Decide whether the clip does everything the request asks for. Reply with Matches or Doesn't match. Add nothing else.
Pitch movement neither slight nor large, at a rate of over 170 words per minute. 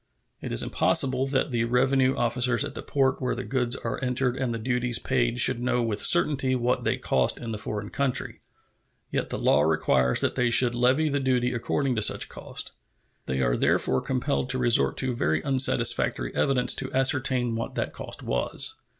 Doesn't match